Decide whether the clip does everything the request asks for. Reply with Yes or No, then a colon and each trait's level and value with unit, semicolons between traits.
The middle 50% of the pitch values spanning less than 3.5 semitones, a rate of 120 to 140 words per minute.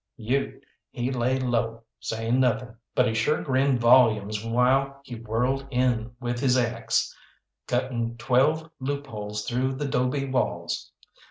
Yes: narrow, 2.5 semitones; slow, 135 wpm